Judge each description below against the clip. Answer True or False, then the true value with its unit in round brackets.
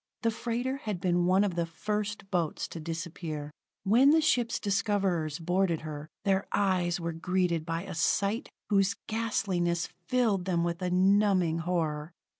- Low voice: False (180 Hz)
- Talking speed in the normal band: True (155 wpm)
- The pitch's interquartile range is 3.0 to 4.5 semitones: True (3.5 semitones)